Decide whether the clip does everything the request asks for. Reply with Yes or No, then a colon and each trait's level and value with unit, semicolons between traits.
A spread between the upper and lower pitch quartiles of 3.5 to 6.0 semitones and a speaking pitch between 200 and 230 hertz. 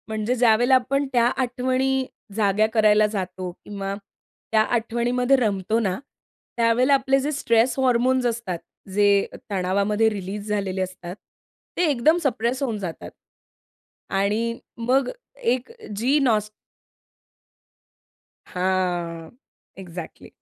Yes: average, 4.2 semitones; high, 220 Hz